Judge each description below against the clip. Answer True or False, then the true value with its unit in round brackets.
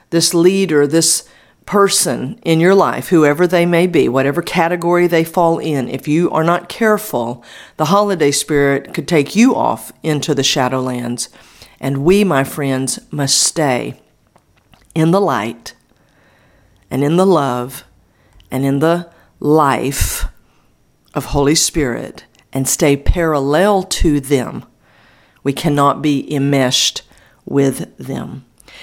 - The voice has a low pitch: False (145 Hz)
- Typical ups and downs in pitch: True (4.2 semitones)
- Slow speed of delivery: True (130 wpm)